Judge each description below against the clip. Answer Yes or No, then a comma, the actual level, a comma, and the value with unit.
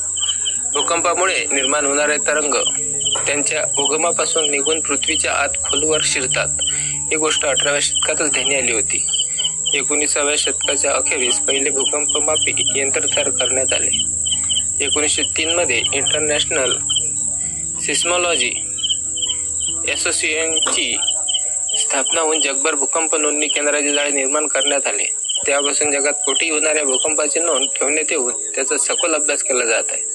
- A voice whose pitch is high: No, medium, 145 Hz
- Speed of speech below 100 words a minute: No, average, 105 wpm